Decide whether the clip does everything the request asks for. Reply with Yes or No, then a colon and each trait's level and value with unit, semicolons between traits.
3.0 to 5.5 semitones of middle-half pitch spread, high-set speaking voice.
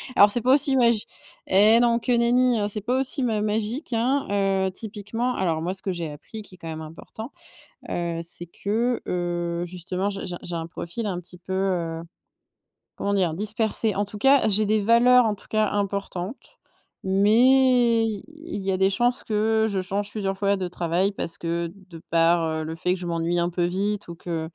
Yes: average, 4.3 semitones; high, 200 Hz